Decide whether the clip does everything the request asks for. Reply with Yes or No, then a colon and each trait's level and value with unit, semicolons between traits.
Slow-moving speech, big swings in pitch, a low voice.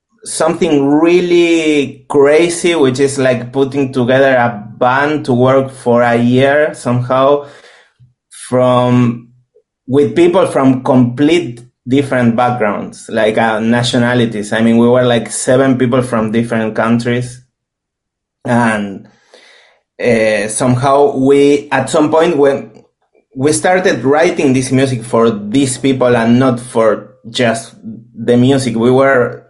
No: slow, 120 wpm; average, 2.8 semitones; low, 125 Hz